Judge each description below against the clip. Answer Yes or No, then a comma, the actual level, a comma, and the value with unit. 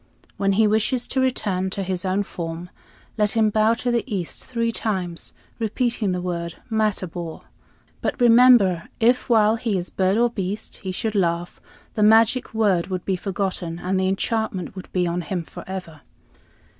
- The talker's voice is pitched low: No, high, 195 Hz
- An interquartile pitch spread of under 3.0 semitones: No, average, 3.6 semitones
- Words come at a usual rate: Yes, average, 170 wpm